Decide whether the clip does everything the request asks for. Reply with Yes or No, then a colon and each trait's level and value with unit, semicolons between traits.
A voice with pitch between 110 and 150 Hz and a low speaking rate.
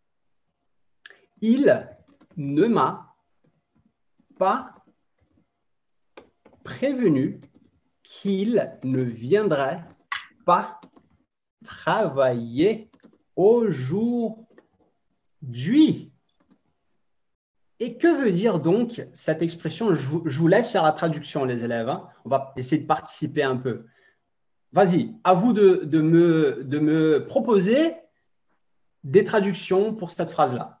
No: medium, 175 Hz; slow, 95 wpm